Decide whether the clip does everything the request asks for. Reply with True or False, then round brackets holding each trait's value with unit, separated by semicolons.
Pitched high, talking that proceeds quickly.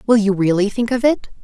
True (215 Hz; 250 wpm)